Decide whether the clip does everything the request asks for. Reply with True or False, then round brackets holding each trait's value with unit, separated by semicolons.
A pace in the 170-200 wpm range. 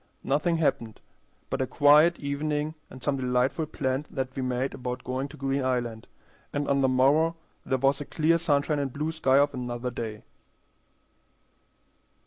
False (160 wpm)